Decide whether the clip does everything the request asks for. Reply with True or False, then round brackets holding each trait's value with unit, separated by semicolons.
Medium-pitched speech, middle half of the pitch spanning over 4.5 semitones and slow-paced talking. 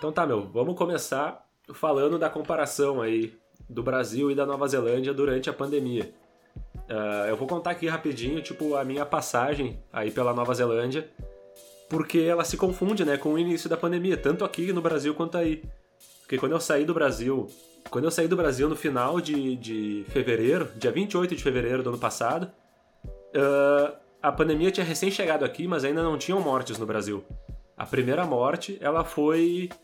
False (145 Hz; 5.3 semitones; 175 wpm)